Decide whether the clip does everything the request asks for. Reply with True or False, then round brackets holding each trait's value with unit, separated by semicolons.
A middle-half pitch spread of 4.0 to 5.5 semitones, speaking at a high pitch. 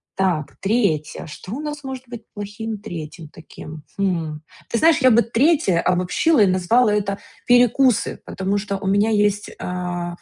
True (4.9 semitones; 205 Hz)